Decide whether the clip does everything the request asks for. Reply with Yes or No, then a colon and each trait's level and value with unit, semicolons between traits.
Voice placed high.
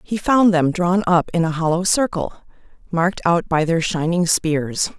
No: medium, 175 Hz